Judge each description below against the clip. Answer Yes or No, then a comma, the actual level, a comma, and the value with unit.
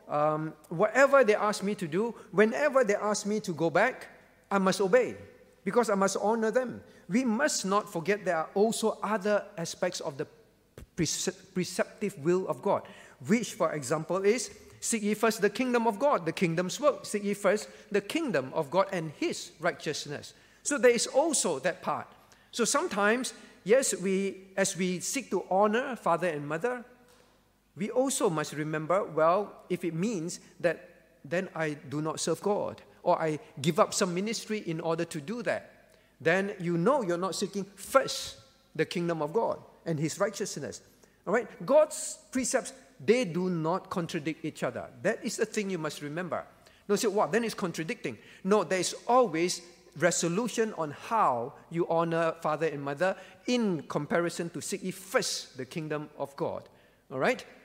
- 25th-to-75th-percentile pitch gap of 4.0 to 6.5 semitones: Yes, average, 4.6 semitones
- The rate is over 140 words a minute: Yes, average, 175 wpm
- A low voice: No, high, 195 Hz